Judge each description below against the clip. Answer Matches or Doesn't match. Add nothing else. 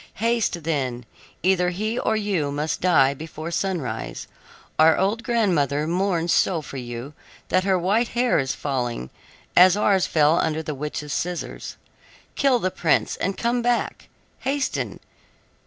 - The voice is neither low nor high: Matches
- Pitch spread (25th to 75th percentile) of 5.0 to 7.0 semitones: Matches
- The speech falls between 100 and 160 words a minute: Matches